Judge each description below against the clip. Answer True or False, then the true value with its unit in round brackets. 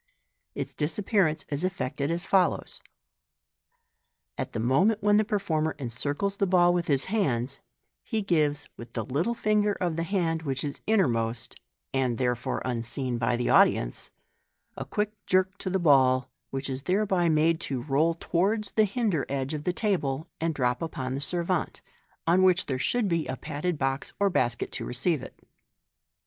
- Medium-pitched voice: True (160 Hz)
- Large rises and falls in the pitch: True (6.0 semitones)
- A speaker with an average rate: True (175 wpm)